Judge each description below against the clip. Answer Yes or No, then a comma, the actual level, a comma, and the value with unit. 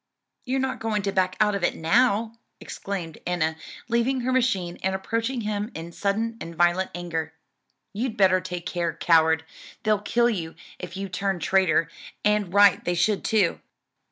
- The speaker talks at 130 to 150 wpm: No, average, 165 wpm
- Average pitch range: Yes, average, 4.0 semitones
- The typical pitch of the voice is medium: No, high, 195 Hz